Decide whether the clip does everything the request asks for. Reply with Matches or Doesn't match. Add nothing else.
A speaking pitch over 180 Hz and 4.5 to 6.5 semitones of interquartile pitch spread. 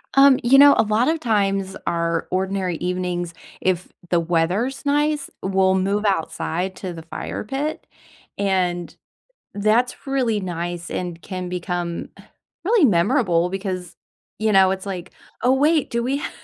Matches